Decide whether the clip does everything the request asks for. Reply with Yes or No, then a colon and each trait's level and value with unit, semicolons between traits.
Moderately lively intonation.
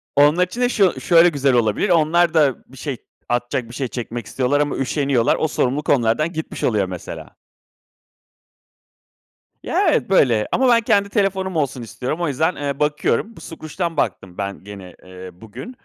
No: wide, 6.1 semitones